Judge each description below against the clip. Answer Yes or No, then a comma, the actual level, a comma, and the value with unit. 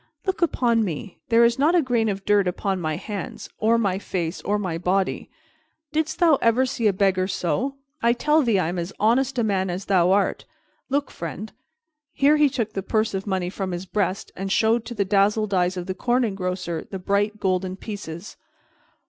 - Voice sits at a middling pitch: No, high, 200 Hz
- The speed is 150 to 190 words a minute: No, average, 200 wpm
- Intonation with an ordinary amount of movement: Yes, average, 3.9 semitones